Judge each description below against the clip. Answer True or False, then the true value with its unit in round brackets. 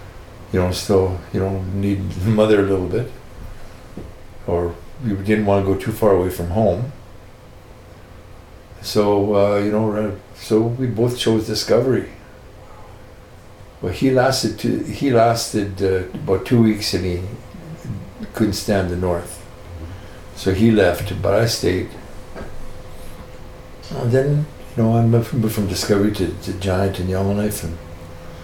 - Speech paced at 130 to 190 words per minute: True (145 wpm)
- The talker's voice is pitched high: False (100 Hz)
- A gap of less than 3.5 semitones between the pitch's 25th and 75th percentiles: True (3.0 semitones)